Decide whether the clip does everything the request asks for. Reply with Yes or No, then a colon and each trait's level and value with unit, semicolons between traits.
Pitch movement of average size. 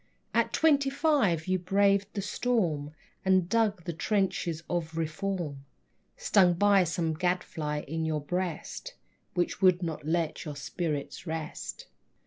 Yes: average, 3.8 semitones